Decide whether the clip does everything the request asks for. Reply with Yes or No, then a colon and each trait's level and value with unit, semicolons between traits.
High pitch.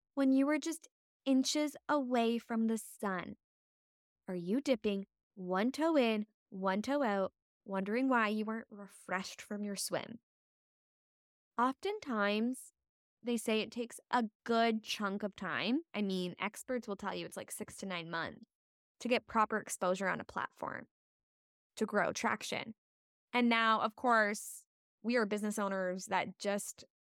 Yes: high, 220 Hz